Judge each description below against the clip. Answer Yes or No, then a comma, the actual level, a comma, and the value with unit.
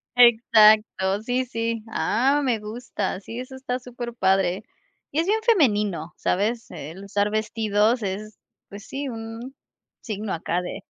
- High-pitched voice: Yes, high, 220 Hz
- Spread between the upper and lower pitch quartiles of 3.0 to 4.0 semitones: Yes, average, 3.4 semitones